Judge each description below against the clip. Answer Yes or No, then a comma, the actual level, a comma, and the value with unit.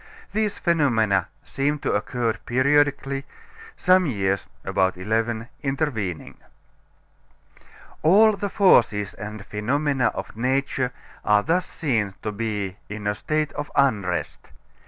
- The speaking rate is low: Yes, slow, 115 wpm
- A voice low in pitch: Yes, low, 120 Hz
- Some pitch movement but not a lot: No, wide, 5.9 semitones